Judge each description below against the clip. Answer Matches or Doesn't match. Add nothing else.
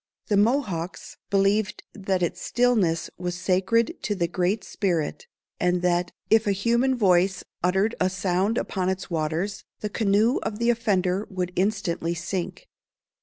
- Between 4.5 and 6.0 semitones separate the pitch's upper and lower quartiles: Doesn't match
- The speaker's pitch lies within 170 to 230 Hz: Matches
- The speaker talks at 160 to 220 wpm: Doesn't match